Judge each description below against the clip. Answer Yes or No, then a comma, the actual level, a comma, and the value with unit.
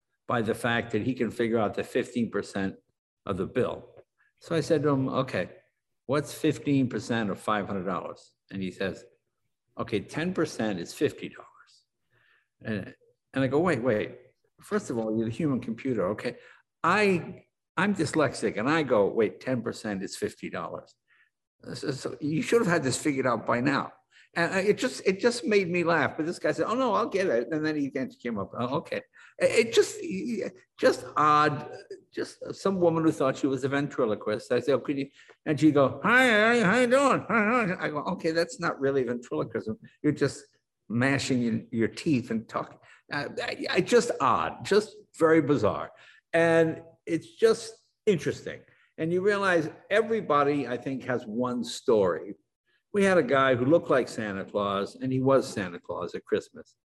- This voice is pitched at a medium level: Yes, medium, 155 Hz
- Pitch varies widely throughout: Yes, wide, 7.3 semitones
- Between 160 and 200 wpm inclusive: Yes, average, 180 wpm